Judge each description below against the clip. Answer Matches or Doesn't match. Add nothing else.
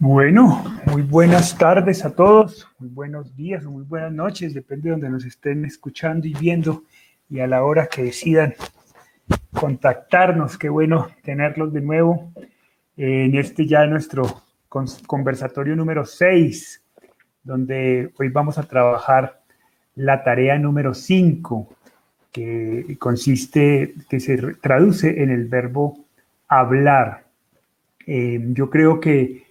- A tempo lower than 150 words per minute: Matches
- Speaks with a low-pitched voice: Doesn't match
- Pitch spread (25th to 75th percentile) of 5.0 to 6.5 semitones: Doesn't match